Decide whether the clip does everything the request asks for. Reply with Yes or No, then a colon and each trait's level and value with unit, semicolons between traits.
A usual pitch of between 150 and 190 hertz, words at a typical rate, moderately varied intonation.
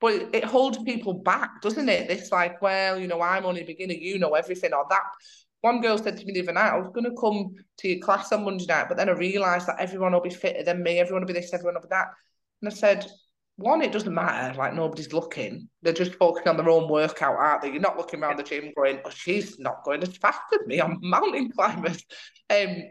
No: medium, 185 Hz; fast, 255 wpm; average, 3.0 semitones